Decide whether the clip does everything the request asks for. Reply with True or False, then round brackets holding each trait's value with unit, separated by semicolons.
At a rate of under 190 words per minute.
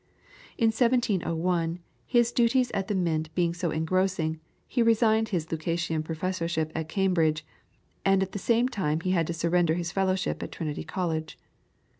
True (155 wpm)